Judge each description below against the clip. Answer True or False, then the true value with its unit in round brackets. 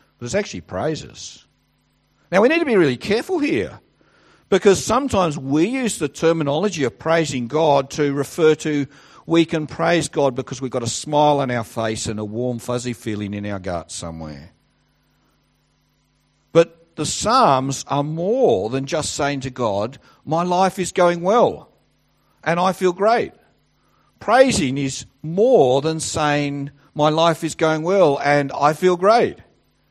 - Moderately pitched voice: True (150 Hz)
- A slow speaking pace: False (155 wpm)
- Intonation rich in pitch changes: False (4.0 semitones)